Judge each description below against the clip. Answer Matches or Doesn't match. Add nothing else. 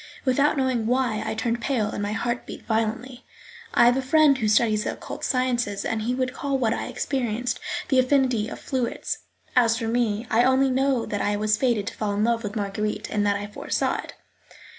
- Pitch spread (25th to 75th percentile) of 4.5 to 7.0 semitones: Doesn't match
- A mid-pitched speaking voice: Doesn't match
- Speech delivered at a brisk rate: Matches